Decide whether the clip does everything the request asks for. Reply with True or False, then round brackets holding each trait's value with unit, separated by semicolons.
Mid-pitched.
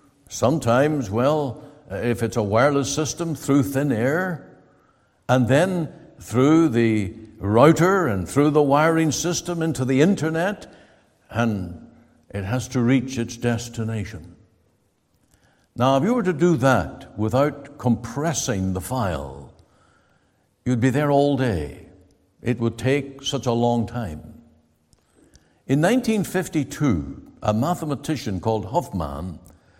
False (130 Hz)